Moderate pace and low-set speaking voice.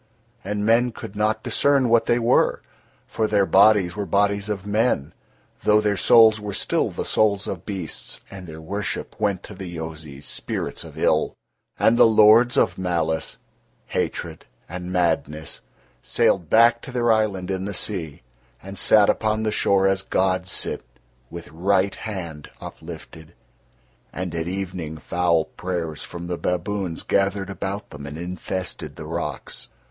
Yes: average, 155 wpm; very low, 95 Hz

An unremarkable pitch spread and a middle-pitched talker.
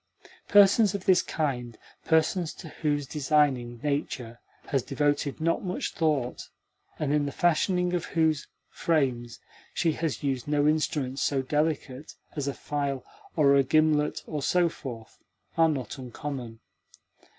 Yes: average, 3.1 semitones; medium, 145 Hz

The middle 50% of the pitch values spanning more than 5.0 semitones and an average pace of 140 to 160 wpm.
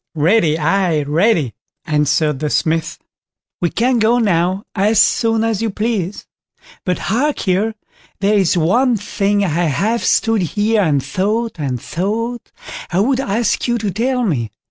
Yes: wide, 5.4 semitones; average, 150 wpm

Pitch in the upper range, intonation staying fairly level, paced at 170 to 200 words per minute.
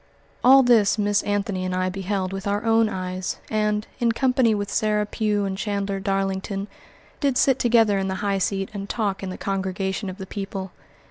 Yes: high, 200 Hz; narrow, 1.8 semitones; average, 190 wpm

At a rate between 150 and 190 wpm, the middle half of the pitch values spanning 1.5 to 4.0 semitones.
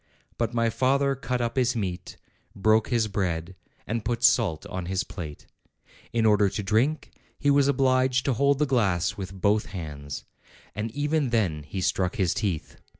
No: average, 170 wpm; wide, 5.5 semitones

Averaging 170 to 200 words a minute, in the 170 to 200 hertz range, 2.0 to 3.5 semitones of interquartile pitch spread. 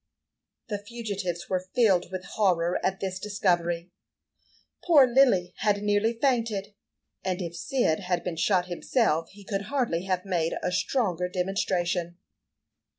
No: slow, 135 wpm; high, 190 Hz; average, 3.0 semitones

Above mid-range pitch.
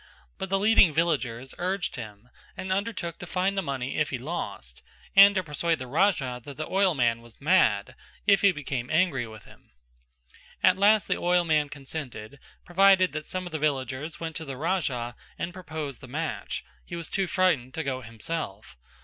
No: medium, 155 Hz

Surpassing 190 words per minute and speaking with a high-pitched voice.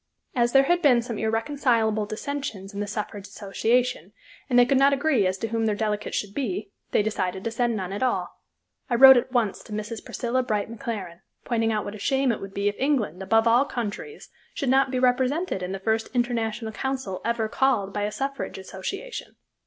Yes: fast, 205 wpm; high, 225 Hz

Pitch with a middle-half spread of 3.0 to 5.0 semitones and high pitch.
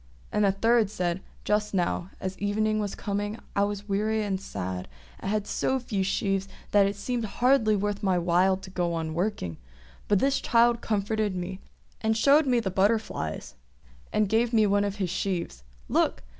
No: narrow, 2.4 semitones; high, 205 Hz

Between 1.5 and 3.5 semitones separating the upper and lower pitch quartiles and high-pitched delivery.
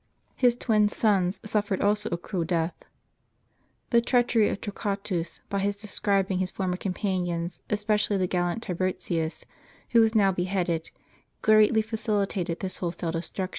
Yes: average, 2.9 semitones; high, 195 Hz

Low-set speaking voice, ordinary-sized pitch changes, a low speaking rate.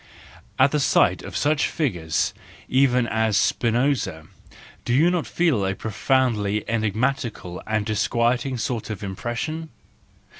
Yes: low, 115 Hz; average, 4.2 semitones; slow, 125 wpm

